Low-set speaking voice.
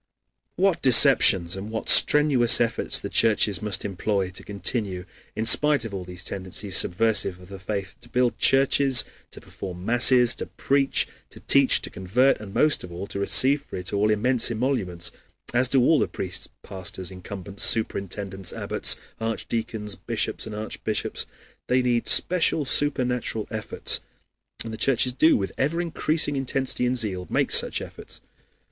Yes: low, 110 Hz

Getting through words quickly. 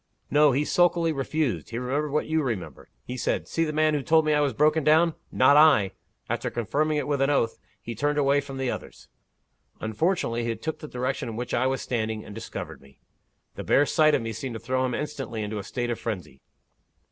Yes: fast, 220 wpm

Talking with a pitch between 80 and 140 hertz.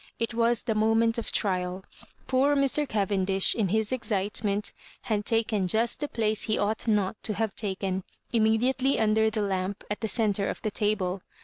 No: high, 215 Hz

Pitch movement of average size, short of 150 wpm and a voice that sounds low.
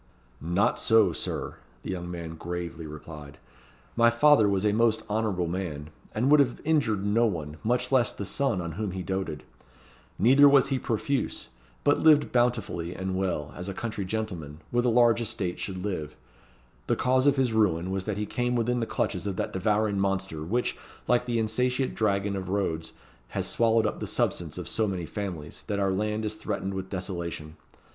No: average, 4.6 semitones; average, 185 wpm; low, 100 Hz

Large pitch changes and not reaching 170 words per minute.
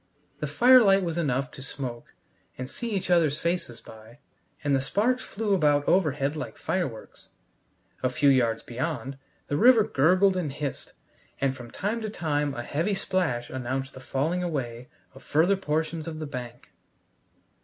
Yes: wide, 5.7 semitones; average, 160 wpm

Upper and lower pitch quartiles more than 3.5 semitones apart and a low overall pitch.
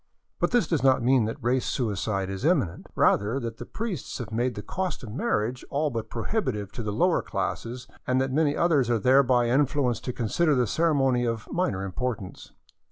Yes: average, 4.2 semitones; low, 125 Hz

